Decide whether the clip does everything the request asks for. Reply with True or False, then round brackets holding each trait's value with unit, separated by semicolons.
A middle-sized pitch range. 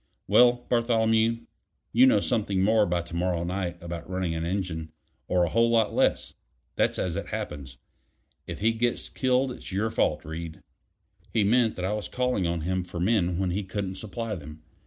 True (4.6 semitones)